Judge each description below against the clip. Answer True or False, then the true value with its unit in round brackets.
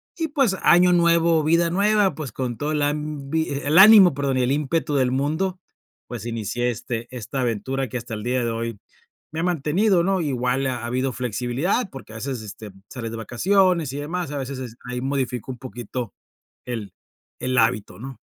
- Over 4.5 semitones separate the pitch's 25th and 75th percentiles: True (5.3 semitones)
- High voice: False (135 Hz)